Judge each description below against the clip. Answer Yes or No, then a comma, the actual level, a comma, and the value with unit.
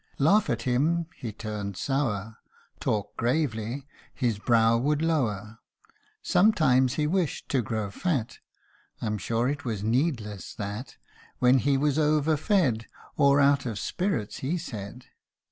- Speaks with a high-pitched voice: No, low, 125 Hz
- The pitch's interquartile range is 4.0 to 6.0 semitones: Yes, average, 5.3 semitones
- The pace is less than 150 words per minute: Yes, slow, 135 wpm